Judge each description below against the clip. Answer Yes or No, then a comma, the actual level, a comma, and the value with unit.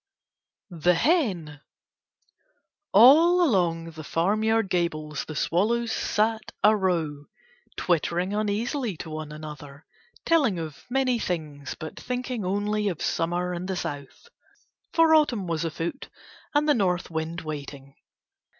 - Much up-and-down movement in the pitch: Yes, wide, 6.0 semitones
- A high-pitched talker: No, medium, 180 Hz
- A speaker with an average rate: No, slow, 125 wpm